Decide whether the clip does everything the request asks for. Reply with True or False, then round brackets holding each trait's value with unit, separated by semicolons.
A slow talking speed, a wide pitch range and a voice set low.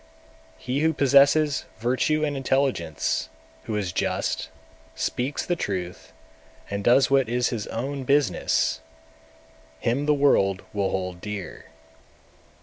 True (125 wpm; 6.0 semitones; 125 Hz)